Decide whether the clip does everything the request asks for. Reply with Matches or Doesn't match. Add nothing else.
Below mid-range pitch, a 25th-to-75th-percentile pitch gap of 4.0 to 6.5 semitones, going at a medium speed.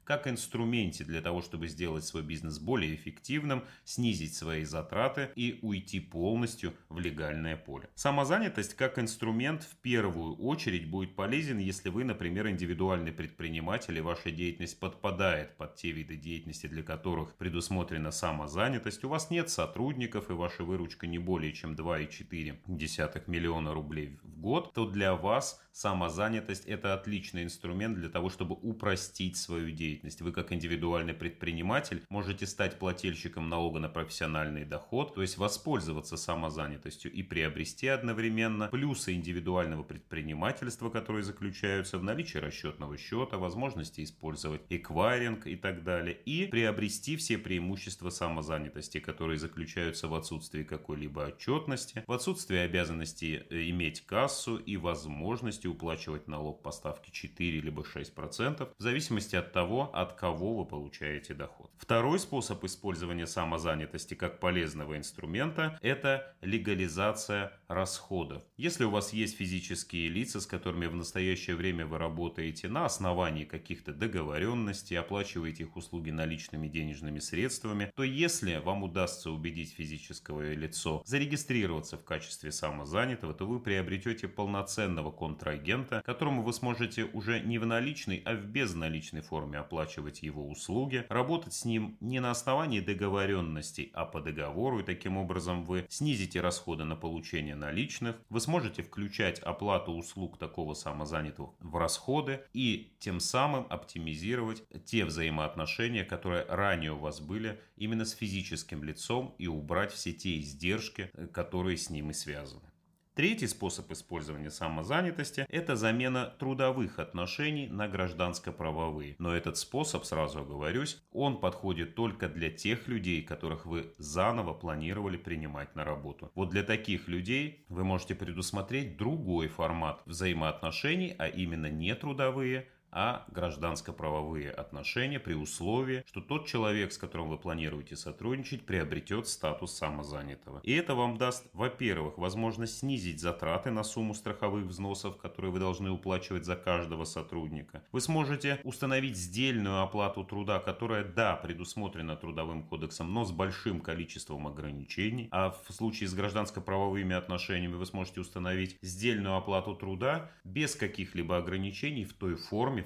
Matches